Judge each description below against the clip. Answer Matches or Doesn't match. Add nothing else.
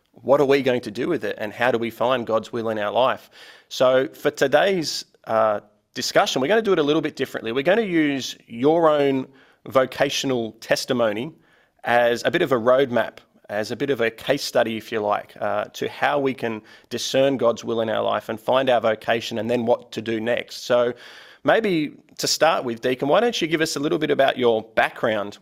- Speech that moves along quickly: Matches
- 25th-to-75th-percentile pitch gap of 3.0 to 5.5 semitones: Matches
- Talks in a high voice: Doesn't match